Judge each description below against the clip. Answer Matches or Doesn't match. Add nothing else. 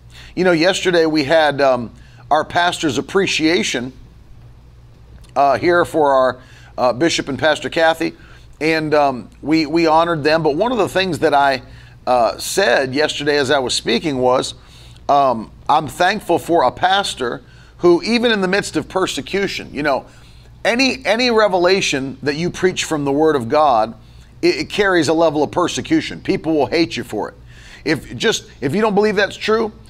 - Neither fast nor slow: Matches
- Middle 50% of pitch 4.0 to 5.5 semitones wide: Matches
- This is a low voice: Doesn't match